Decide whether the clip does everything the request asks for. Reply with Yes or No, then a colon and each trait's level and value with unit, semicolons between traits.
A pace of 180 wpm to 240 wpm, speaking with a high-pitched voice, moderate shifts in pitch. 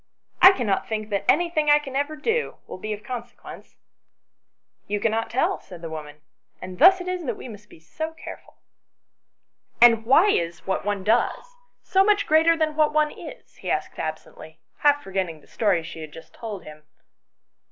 No: average, 200 wpm; high, 230 Hz; wide, 8.4 semitones